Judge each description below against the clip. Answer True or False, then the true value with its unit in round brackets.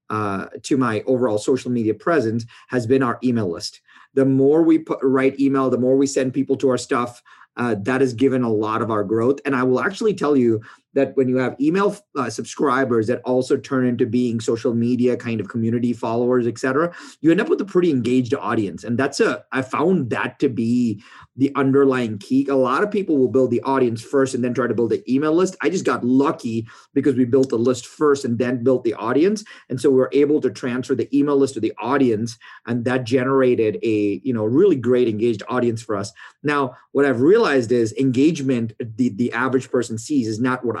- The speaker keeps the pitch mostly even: True (2.3 semitones)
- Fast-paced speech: True (220 wpm)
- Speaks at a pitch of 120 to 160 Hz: True (130 Hz)